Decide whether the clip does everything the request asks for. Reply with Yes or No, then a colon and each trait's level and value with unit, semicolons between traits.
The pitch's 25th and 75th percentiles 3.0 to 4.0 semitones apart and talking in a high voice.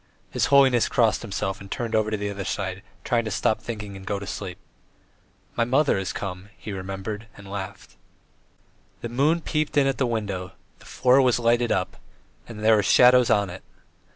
No: average, 3.7 semitones; low, 105 Hz